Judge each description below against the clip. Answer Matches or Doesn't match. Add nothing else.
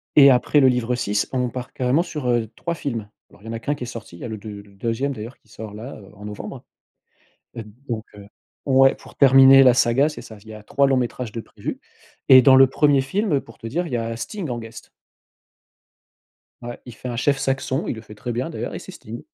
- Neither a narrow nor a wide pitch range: Matches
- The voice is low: Matches